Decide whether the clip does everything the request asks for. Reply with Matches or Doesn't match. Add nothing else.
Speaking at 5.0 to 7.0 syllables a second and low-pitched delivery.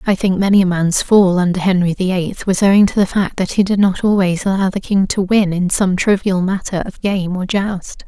Doesn't match